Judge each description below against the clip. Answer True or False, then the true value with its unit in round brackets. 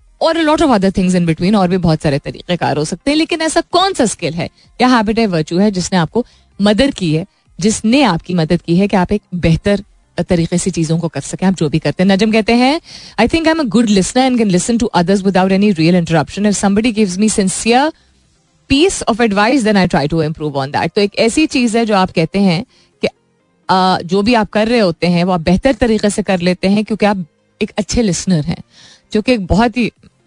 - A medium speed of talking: False (230 wpm)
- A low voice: False (200 Hz)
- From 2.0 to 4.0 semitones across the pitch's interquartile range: False (4.7 semitones)